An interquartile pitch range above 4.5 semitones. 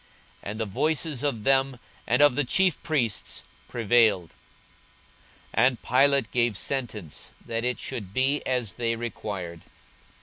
No: average, 3.8 semitones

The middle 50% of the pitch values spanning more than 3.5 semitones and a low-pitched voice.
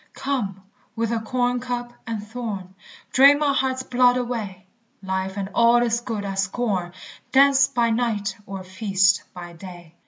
No: average, 4.3 semitones; high, 225 Hz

